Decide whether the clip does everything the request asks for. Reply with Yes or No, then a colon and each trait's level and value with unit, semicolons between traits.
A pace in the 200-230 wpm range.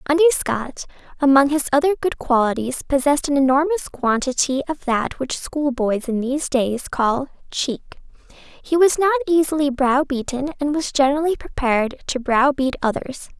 No: average, 145 wpm